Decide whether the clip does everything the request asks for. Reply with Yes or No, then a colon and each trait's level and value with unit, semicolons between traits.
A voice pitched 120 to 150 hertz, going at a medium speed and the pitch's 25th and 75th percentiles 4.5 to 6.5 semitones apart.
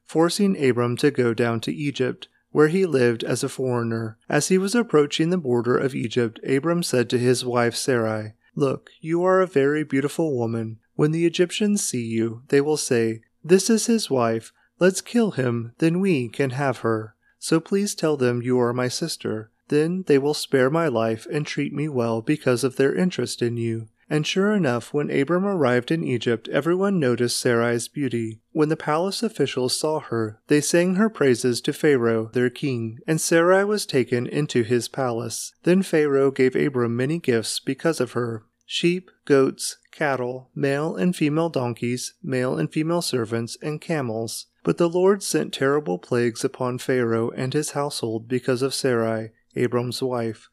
Yes: low, 135 Hz; average, 175 wpm; average, 5.1 semitones